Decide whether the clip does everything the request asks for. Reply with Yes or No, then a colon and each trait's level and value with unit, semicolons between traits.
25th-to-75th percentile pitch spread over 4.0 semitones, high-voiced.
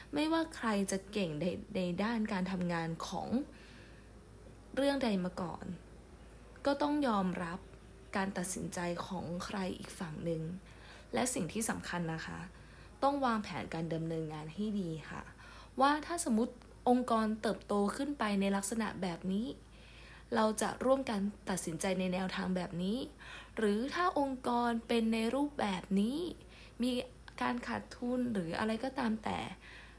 Yes: average, 5.2 semitones; high, 205 Hz